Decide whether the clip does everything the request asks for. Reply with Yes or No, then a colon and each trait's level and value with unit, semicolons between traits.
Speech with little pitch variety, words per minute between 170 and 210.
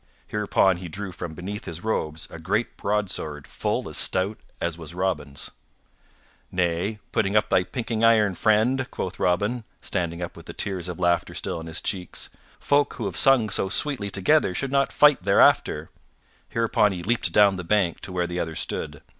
No: average, 3.8 semitones; average, 180 wpm